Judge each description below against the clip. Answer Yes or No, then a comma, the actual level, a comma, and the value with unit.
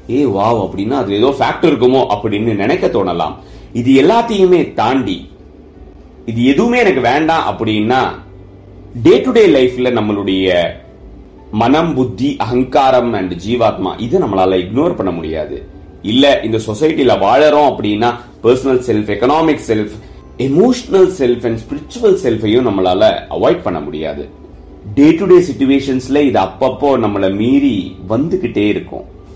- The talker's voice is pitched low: Yes, low, 120 Hz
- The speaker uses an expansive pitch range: Yes, wide, 6.0 semitones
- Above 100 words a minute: Yes, average, 110 wpm